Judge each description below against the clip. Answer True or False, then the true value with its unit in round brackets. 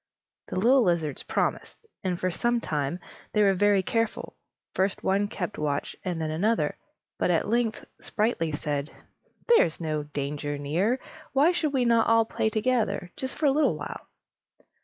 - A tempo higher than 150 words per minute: True (165 wpm)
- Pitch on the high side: True (195 Hz)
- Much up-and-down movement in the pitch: True (6.9 semitones)